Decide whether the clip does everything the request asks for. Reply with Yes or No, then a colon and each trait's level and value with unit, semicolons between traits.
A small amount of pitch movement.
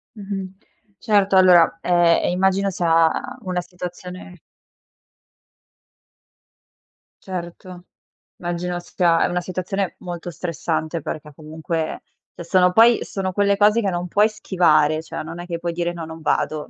Yes: narrow, 2.0 semitones